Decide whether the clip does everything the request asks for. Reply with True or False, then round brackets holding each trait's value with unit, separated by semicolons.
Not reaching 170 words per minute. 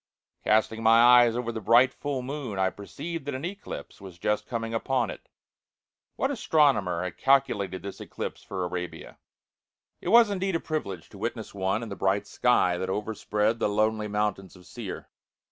False (180 wpm)